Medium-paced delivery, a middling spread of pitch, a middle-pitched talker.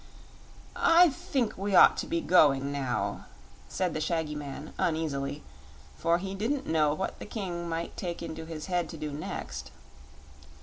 Yes: average, 160 wpm; average, 3.5 semitones; medium, 165 Hz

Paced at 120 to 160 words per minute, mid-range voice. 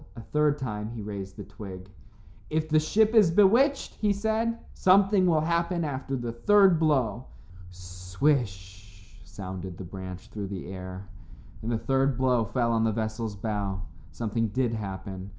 No: average, 155 wpm; low, 115 Hz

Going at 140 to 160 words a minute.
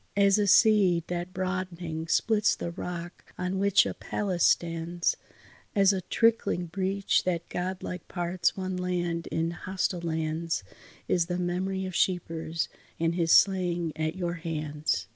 Yes: average, 145 wpm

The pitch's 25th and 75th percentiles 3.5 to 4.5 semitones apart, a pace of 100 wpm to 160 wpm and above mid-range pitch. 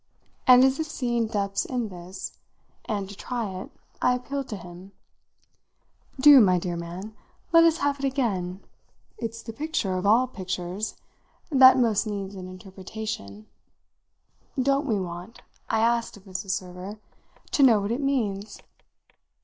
No: average, 5.1 semitones; average, 150 wpm; high, 215 Hz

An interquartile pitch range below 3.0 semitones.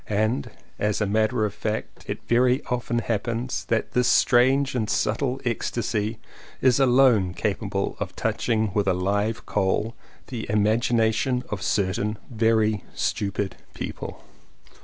Yes: narrow, 2.6 semitones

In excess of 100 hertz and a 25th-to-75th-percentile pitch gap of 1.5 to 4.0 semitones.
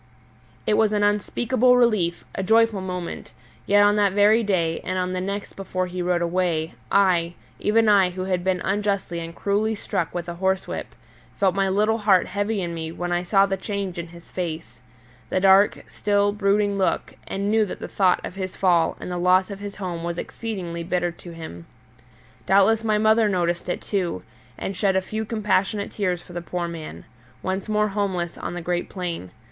Yes: high, 190 Hz; average, 2.8 semitones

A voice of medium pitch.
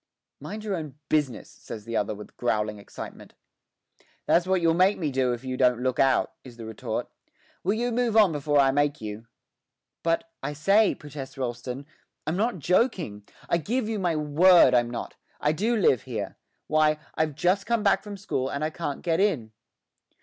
Yes: medium, 150 Hz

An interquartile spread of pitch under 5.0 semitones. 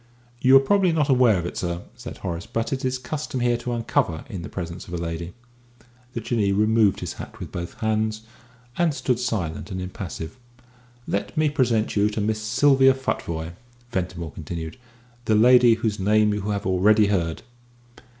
No: average, 5.3 semitones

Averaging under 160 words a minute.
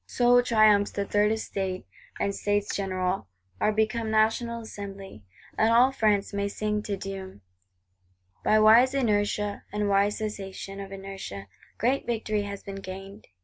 Yes: average, 145 wpm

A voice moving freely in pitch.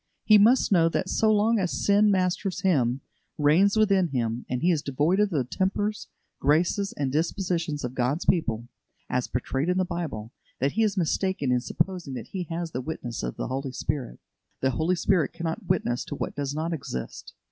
Yes: wide, 6.0 semitones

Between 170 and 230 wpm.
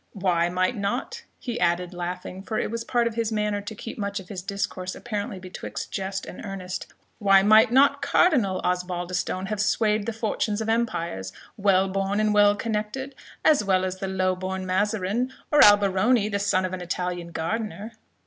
Yes: average, 180 wpm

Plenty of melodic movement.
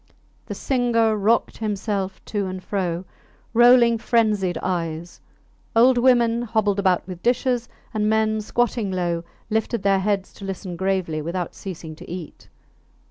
No: average, 3.8 semitones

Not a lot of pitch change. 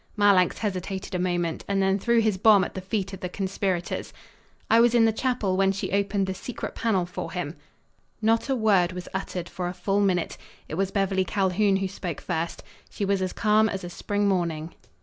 Yes: narrow, 2.1 semitones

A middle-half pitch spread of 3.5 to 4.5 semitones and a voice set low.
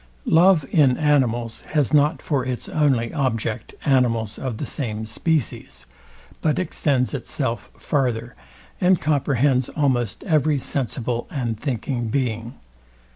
Yes: average, 4.0 semitones; low, 130 Hz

